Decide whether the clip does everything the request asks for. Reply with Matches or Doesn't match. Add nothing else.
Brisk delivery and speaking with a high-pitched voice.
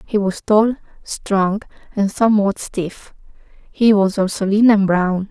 Doesn't match